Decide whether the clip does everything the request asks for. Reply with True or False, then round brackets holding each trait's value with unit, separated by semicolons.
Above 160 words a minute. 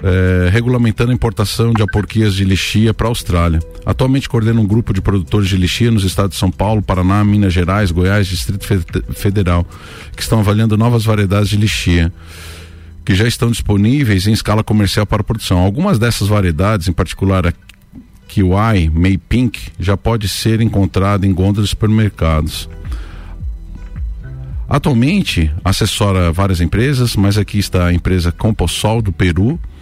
False (155 wpm)